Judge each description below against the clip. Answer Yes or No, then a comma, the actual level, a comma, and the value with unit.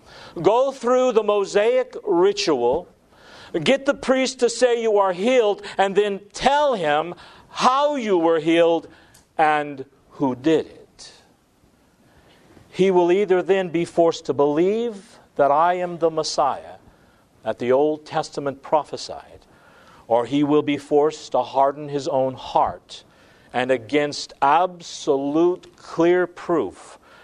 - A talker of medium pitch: Yes, medium, 170 Hz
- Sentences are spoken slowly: Yes, slow, 130 wpm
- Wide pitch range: Yes, wide, 6.5 semitones